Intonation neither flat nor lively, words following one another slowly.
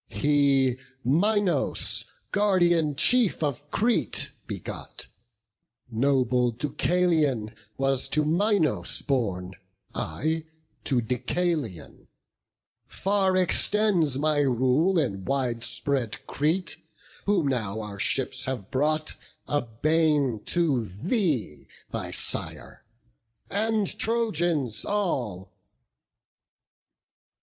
No: wide, 5.9 semitones; slow, 85 wpm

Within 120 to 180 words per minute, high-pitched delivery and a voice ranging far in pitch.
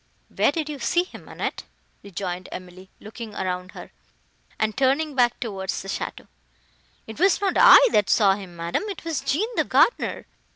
Yes: average, 170 wpm; high, 220 Hz; wide, 8.2 semitones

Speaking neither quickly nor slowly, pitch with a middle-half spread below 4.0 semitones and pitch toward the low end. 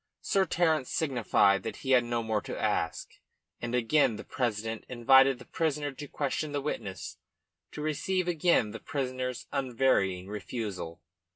No: average, 150 wpm; average, 4.8 semitones; low, 125 Hz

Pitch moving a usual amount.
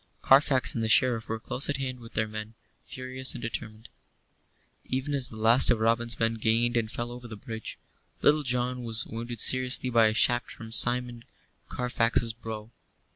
No: narrow, 2.0 semitones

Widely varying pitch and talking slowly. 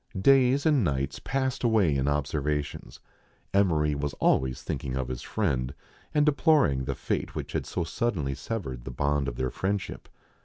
No: wide, 8.9 semitones; average, 165 wpm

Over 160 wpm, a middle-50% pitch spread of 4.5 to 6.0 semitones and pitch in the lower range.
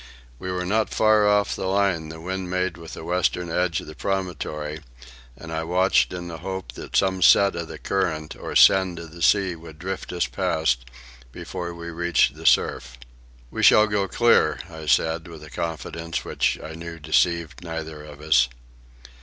No: average, 185 wpm; average, 2.8 semitones; very low, 85 Hz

